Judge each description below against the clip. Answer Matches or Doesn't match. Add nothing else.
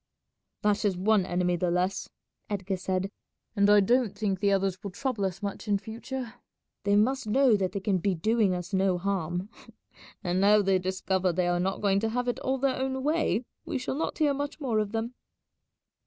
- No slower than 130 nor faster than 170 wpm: Doesn't match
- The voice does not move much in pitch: Doesn't match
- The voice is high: Matches